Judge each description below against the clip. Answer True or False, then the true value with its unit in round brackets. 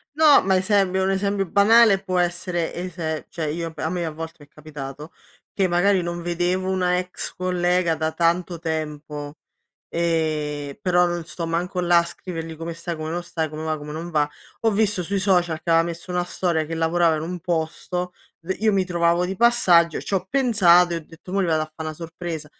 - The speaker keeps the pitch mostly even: True (2.2 semitones)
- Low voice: False (175 Hz)